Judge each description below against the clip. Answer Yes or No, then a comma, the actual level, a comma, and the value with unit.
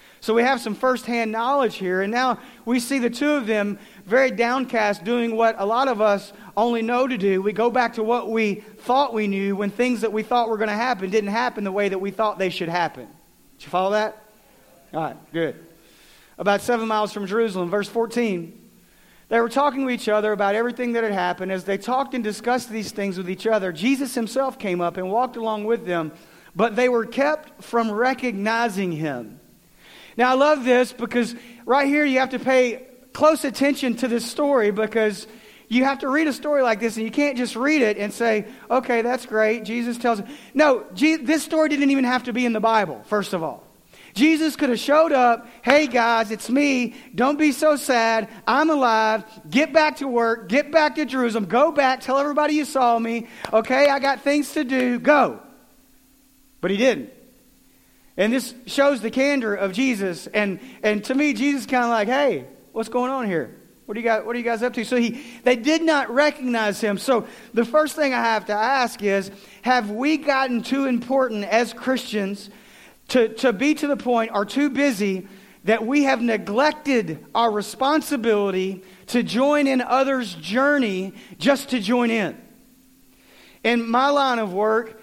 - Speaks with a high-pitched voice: Yes, high, 235 Hz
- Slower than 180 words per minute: No, average, 200 wpm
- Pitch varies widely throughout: No, average, 3.6 semitones